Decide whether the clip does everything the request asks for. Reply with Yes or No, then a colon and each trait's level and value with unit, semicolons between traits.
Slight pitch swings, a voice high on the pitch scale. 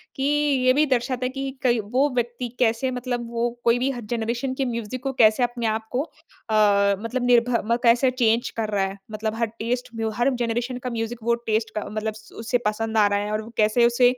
Yes: narrow, 2.3 semitones; high, 240 Hz